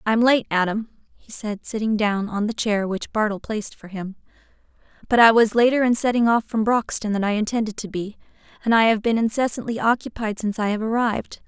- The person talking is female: Yes, female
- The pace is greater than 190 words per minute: Yes, average, 200 wpm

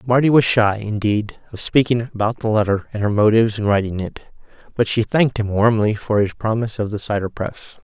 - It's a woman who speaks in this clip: No, male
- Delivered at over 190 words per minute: Yes, fast, 205 wpm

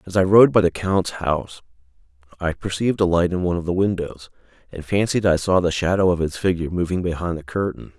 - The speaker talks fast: Yes, fast, 220 wpm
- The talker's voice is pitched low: Yes, very low, 90 Hz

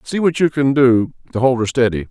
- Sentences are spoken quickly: Yes, fast, 255 wpm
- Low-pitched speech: Yes, low, 130 Hz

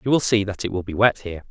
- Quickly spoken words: Yes, fast, 360 wpm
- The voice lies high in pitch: No, low, 105 Hz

